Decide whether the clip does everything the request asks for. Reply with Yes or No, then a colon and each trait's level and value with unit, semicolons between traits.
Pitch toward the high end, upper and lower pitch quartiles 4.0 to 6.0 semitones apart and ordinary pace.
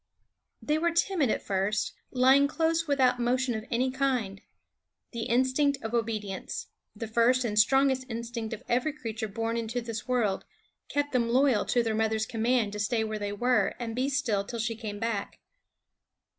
No: high, 235 Hz; average, 3.0 semitones; average, 170 wpm